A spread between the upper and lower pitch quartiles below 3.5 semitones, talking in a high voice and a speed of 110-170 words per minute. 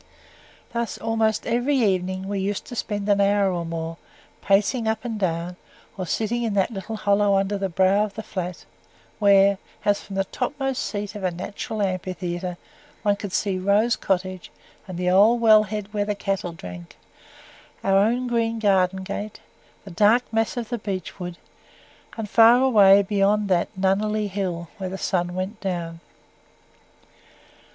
Yes: narrow, 2.5 semitones; high, 200 Hz; average, 165 wpm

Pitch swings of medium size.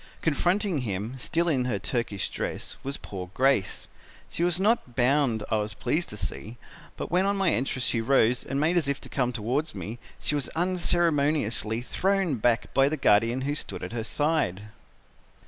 No: wide, 6.0 semitones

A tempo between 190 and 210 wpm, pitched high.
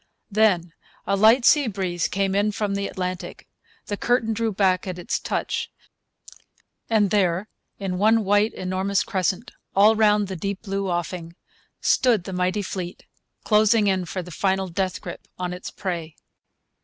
No: average, 155 wpm; high, 195 Hz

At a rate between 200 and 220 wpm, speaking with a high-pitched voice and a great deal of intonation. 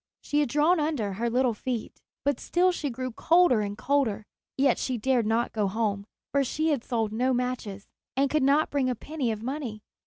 No: fast, 205 wpm; very high, 255 Hz; average, 4.3 semitones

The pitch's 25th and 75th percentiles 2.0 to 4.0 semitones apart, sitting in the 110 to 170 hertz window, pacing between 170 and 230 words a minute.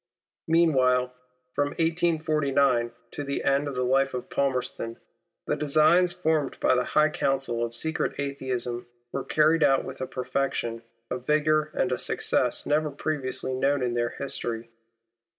No: average, 3.3 semitones; medium, 140 Hz; average, 150 wpm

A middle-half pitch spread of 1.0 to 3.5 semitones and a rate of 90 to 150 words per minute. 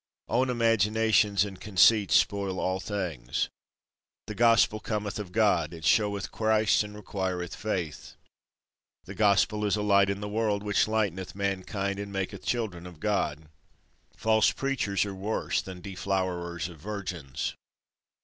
Yes: narrow, 2.5 semitones; average, 140 wpm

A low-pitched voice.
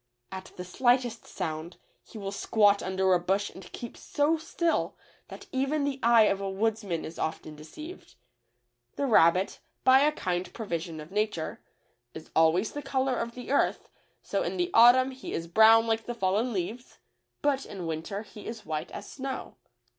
No: high, 215 Hz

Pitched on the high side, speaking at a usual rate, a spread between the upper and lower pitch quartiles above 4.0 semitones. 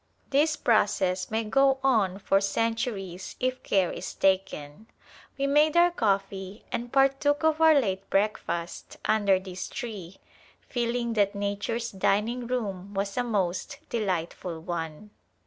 No: high, 210 Hz; slow, 130 wpm; average, 4.4 semitones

